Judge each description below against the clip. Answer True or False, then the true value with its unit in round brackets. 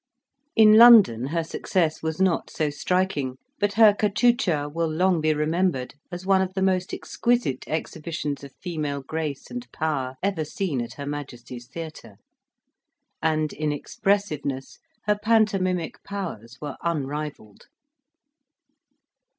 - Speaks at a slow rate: True (125 wpm)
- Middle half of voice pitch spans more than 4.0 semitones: True (4.8 semitones)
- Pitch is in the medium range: True (160 Hz)